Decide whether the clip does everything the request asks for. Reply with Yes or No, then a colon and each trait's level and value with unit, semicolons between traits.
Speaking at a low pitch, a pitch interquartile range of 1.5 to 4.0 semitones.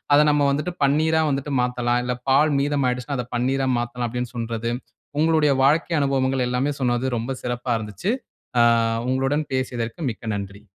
Yes: low, 130 Hz; average, 2.9 semitones